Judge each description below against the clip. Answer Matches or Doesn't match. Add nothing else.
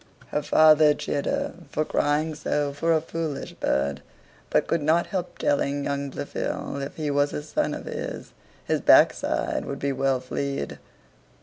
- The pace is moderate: Matches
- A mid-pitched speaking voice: Matches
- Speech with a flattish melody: Matches